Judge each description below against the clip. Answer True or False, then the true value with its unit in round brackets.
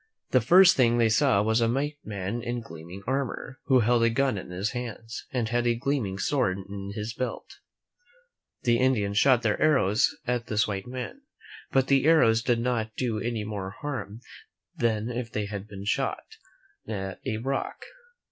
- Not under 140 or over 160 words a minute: False (175 wpm)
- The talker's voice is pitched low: True (115 Hz)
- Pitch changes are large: False (3.5 semitones)